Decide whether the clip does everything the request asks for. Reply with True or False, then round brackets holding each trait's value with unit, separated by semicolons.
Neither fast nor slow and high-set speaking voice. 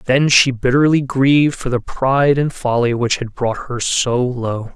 False (190 wpm; 130 Hz)